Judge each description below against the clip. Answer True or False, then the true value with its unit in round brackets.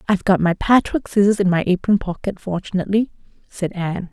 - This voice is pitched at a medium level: False (195 Hz)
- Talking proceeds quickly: False (175 wpm)